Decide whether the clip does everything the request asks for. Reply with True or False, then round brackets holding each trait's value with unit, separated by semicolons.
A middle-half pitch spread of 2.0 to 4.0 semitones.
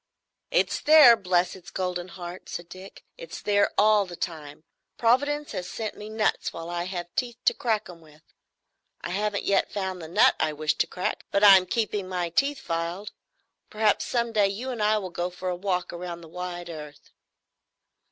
True (3.5 semitones)